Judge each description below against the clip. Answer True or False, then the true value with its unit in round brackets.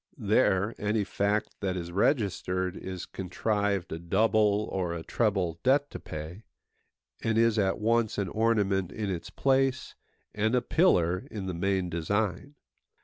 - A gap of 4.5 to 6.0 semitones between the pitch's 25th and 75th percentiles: False (3.4 semitones)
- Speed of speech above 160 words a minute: False (145 wpm)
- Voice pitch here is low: True (100 Hz)